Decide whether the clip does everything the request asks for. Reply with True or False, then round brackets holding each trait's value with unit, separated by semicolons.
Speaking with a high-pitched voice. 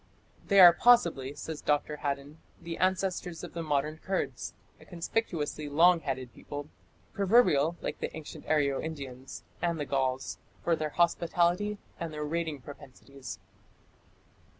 False (155 Hz)